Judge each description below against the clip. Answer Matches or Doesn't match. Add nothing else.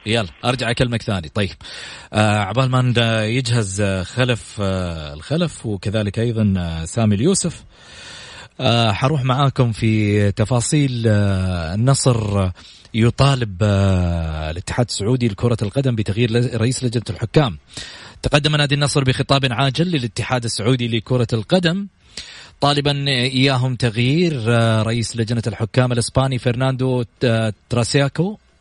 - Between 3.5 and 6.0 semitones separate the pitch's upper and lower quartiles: Matches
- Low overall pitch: Matches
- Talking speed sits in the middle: Doesn't match